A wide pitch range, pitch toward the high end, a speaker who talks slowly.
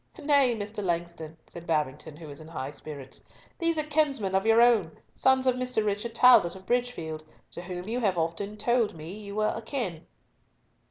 No: wide, 6.7 semitones; high, 205 Hz; average, 180 wpm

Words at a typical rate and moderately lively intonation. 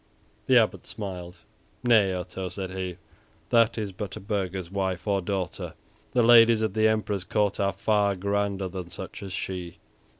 No: average, 165 wpm; narrow, 2.2 semitones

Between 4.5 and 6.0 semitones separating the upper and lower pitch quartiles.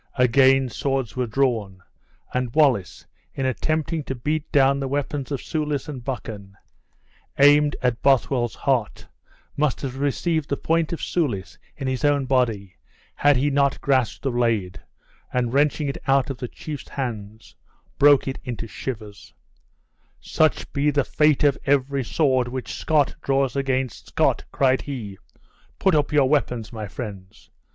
No: average, 3.0 semitones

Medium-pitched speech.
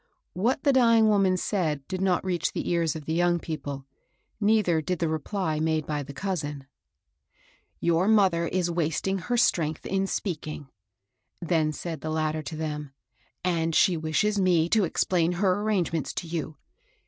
Yes: medium, 170 Hz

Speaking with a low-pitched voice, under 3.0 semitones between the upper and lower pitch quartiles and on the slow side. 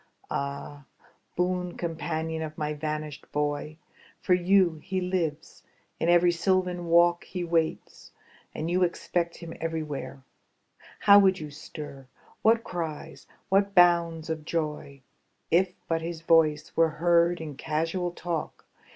No: medium, 165 Hz; narrow, 2.4 semitones; slow, 130 wpm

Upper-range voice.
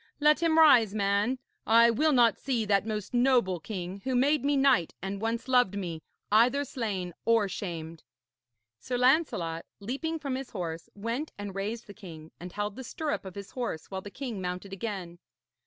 Yes: high, 215 Hz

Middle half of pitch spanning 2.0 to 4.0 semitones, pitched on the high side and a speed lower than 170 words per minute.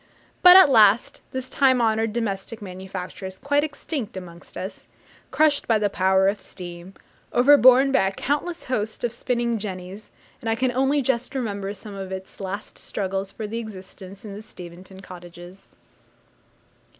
No: average, 4.8 semitones; high, 210 Hz; average, 155 wpm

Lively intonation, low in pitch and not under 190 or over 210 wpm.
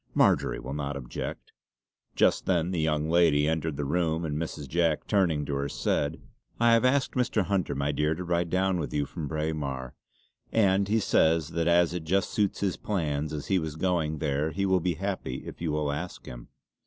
No: average, 3.9 semitones; very low, 80 Hz; fast, 205 wpm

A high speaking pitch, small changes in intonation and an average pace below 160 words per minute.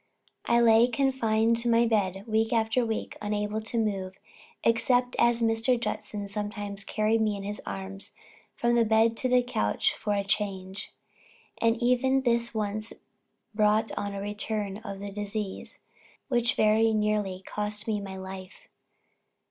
Yes: high, 215 Hz; narrow, 2.2 semitones; average, 150 wpm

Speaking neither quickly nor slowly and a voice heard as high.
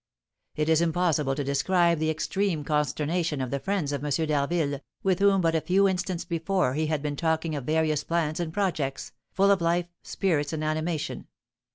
No: average, 185 wpm; medium, 160 Hz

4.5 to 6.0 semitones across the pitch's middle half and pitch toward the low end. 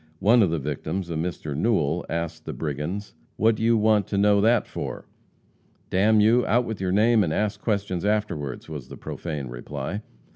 Yes: average, 5.2 semitones; low, 100 Hz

